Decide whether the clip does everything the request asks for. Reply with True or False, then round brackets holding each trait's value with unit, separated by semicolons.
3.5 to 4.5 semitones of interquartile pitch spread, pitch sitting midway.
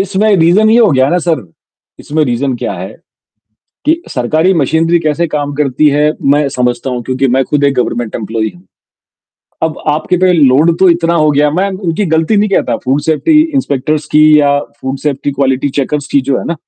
True (4.1 semitones; 150 Hz)